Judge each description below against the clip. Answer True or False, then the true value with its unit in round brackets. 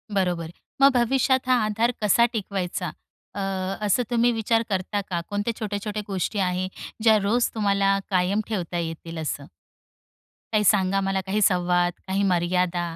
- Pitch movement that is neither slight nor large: True (3.1 semitones)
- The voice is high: True (195 Hz)